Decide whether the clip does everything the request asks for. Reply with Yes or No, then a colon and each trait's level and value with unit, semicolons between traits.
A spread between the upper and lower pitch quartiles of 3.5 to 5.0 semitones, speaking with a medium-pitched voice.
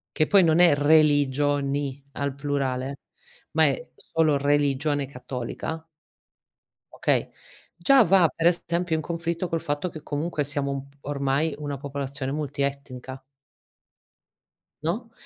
No: average, 2.7 semitones; medium, 145 Hz